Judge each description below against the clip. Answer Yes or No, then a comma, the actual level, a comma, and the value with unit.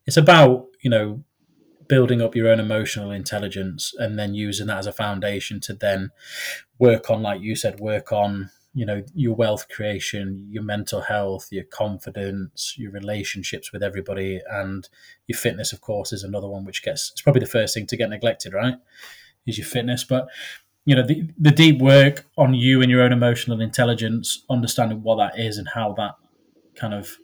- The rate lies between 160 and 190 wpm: Yes, average, 185 wpm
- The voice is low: Yes, low, 110 Hz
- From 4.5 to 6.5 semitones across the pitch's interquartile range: No, average, 3.5 semitones